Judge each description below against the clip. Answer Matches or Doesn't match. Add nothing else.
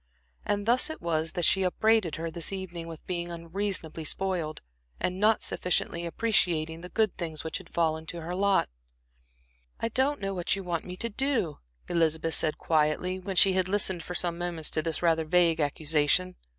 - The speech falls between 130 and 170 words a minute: Doesn't match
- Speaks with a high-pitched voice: Doesn't match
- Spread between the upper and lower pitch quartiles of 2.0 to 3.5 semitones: Matches